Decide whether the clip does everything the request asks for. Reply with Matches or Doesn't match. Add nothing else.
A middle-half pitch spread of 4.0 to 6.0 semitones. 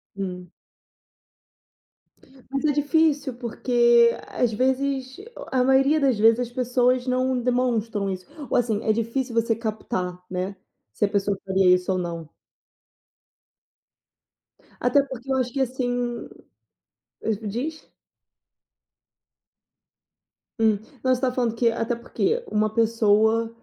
Doesn't match